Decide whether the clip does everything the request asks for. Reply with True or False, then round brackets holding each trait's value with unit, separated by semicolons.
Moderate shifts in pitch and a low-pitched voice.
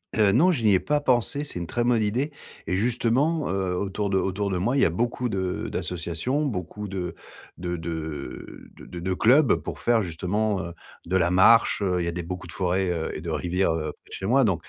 True (5.0 semitones; 95 Hz)